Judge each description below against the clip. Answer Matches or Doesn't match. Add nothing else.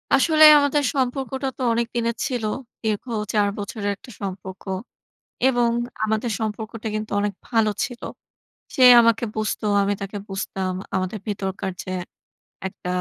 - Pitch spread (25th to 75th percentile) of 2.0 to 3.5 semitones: Matches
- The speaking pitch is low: Doesn't match